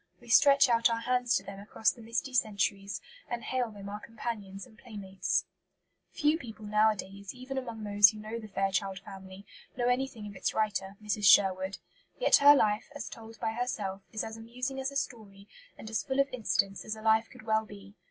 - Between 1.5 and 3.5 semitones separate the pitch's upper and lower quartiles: Yes, average, 3.2 semitones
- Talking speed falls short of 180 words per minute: No, average, 200 wpm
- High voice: Yes, high, 220 Hz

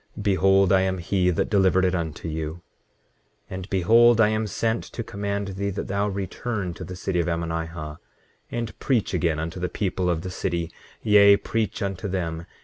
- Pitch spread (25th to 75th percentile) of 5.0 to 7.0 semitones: No, average, 2.9 semitones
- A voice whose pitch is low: Yes, very low, 95 Hz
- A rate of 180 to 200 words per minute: Yes, average, 185 wpm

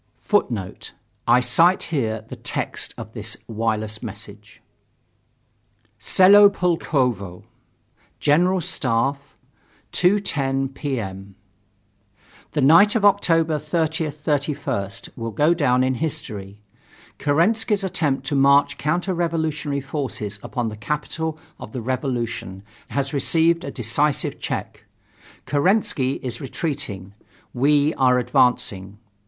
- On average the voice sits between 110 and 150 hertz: Yes, medium, 140 Hz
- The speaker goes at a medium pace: No, slow, 105 wpm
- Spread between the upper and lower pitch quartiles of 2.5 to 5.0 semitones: No, wide, 5.4 semitones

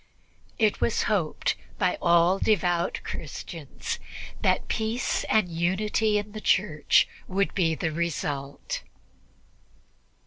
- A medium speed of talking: No, slow, 105 wpm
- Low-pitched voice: No, medium, 185 Hz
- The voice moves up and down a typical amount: Yes, average, 3.9 semitones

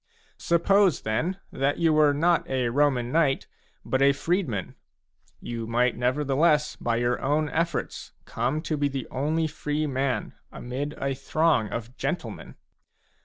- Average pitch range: Yes, average, 3.8 semitones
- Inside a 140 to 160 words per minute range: Yes, average, 150 wpm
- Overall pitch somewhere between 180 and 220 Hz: No, medium, 140 Hz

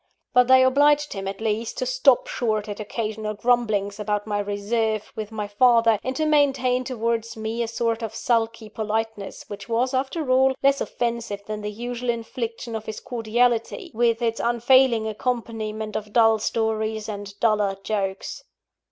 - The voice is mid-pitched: No, high, 225 Hz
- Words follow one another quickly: No, average, 160 wpm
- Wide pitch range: No, narrow, 2.4 semitones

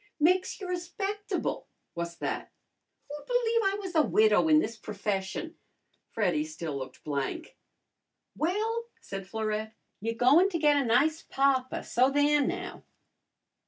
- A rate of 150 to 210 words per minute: No, slow, 135 wpm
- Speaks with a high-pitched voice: Yes, very high, 285 Hz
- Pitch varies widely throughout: Yes, wide, 9.0 semitones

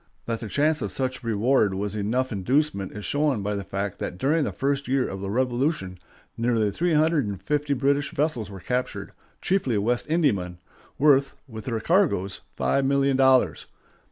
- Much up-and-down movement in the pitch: Yes, wide, 5.7 semitones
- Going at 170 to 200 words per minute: Yes, average, 175 wpm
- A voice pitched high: No, low, 125 Hz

